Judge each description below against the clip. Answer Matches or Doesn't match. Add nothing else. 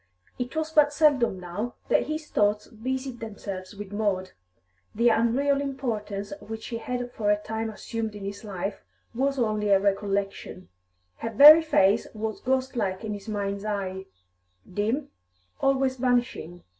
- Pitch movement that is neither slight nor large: Matches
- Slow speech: Doesn't match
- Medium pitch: Doesn't match